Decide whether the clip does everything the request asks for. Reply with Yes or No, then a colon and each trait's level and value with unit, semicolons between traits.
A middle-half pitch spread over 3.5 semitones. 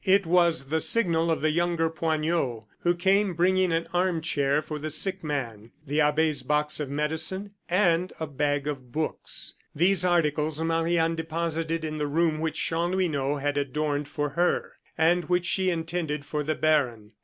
No: narrow, 2.6 semitones